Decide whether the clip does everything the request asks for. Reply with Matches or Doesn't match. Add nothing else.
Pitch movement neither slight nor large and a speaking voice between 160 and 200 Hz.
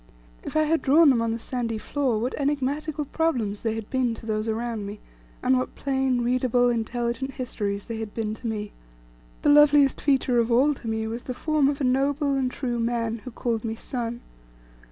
Doesn't match